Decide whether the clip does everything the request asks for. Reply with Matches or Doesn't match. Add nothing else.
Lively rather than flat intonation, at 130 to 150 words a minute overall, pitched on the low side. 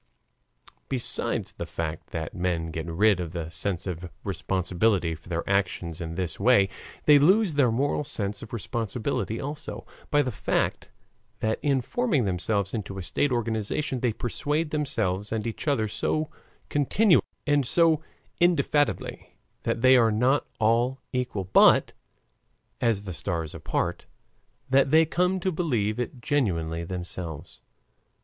Matches